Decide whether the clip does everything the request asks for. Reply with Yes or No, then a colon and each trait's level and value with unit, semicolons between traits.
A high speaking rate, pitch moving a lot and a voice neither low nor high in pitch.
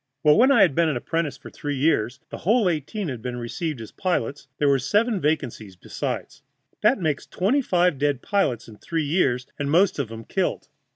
Yes: fast, 210 wpm; wide, 5.8 semitones; medium, 150 Hz